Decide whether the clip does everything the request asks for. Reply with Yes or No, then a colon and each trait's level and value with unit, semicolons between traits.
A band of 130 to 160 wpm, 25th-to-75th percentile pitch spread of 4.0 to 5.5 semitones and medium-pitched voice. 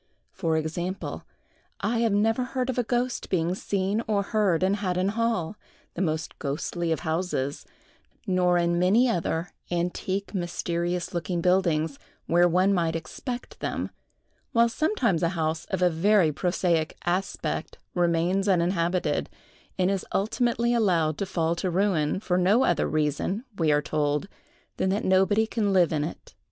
No: average, 150 wpm; average, 3.3 semitones; medium, 180 Hz